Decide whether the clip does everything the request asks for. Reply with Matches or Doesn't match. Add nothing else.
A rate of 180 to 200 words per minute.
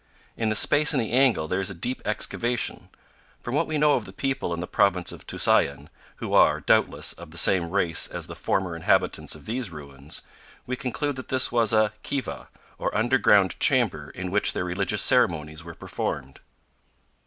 Matches